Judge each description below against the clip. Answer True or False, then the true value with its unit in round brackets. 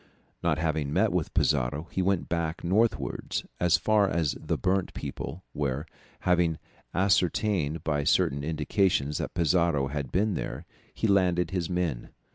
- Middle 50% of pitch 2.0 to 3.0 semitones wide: False (3.8 semitones)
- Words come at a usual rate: True (145 wpm)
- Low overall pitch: True (85 Hz)